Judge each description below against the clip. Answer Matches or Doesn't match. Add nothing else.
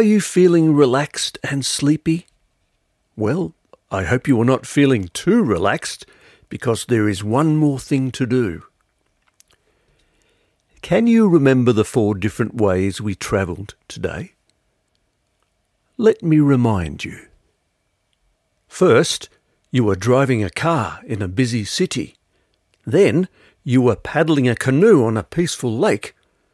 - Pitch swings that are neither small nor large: Doesn't match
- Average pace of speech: Doesn't match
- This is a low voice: Matches